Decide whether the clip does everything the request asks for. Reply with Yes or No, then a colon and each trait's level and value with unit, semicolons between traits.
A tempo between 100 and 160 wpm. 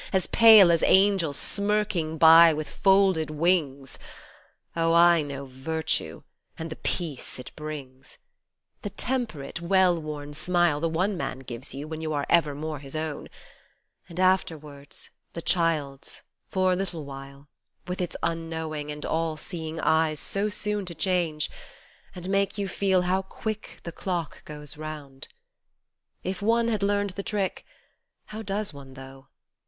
Yes: average, 150 wpm